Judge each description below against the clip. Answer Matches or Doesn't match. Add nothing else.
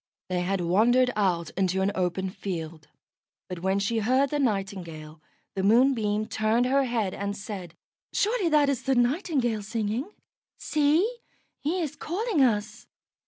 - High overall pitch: Matches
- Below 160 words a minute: Matches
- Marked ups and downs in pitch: Matches